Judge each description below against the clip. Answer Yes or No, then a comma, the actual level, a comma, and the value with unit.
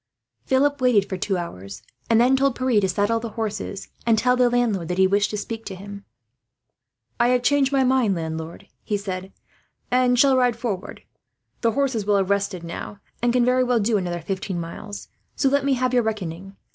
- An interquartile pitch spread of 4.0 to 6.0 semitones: Yes, average, 4.5 semitones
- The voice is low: No, high, 220 Hz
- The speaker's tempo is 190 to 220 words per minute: Yes, average, 200 wpm